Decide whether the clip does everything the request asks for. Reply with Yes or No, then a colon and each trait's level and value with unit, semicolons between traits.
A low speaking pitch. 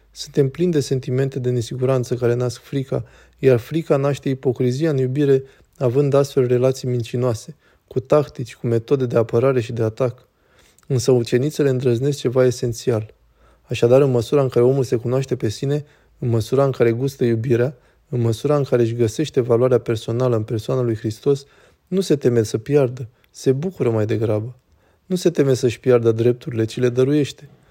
Yes: low, 125 Hz